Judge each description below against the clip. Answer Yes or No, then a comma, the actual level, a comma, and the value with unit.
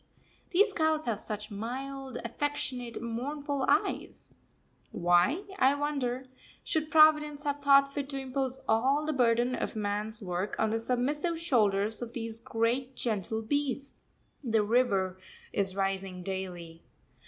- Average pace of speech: No, slow, 130 wpm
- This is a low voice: No, high, 245 Hz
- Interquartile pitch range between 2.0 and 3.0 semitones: No, average, 5.1 semitones